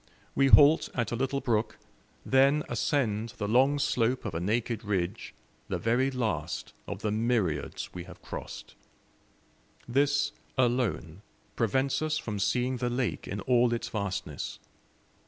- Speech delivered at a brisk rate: No, average, 140 wpm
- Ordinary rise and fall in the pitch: Yes, average, 4.3 semitones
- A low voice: Yes, low, 120 Hz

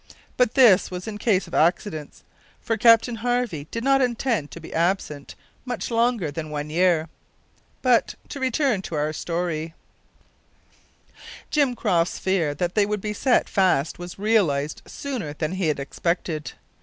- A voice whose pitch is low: No, medium, 185 Hz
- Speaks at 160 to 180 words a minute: No, average, 150 wpm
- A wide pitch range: Yes, wide, 6.6 semitones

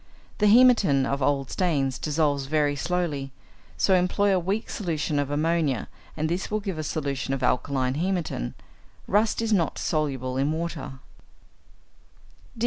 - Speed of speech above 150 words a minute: No, average, 140 wpm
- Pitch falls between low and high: Yes, medium, 155 Hz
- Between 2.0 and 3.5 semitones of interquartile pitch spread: No, average, 4.8 semitones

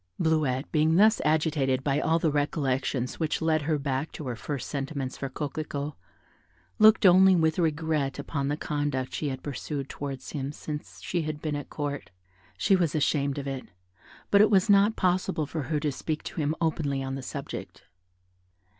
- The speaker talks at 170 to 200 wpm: Yes, average, 180 wpm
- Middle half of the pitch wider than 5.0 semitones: No, average, 2.7 semitones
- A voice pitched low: No, medium, 150 Hz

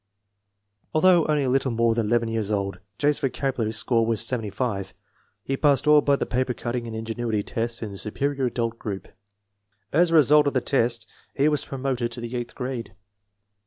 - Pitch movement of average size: Yes, average, 3.4 semitones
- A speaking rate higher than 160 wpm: Yes, average, 185 wpm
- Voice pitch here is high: No, low, 120 Hz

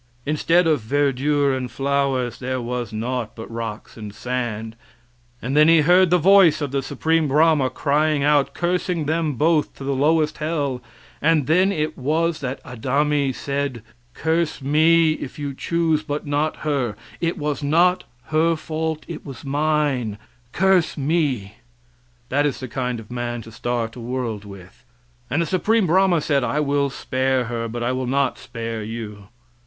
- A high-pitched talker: No, medium, 140 Hz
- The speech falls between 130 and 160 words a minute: No, average, 170 wpm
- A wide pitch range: No, average, 4.1 semitones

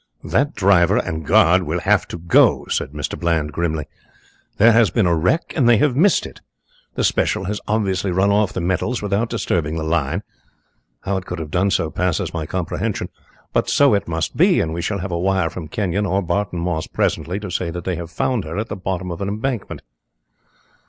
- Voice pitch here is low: Yes, very low, 90 Hz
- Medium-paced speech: No, fast, 210 wpm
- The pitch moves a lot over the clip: No, average, 3.5 semitones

